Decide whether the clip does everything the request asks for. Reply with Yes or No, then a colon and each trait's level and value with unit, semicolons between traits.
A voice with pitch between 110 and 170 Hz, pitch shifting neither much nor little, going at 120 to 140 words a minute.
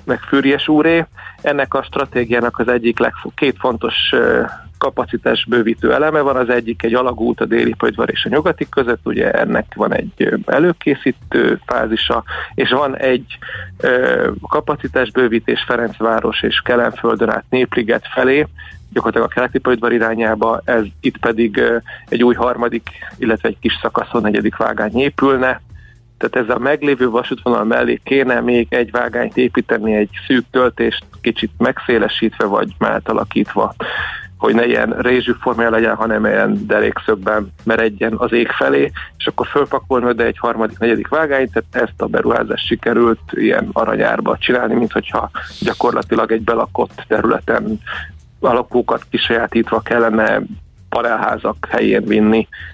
No: low, 120 Hz; narrow, 2.0 semitones; average, 135 wpm